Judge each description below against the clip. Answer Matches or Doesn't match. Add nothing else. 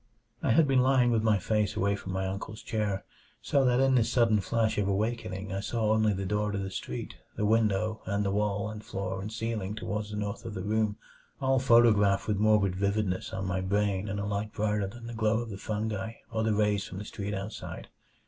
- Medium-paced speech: Doesn't match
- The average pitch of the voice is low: Matches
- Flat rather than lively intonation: Matches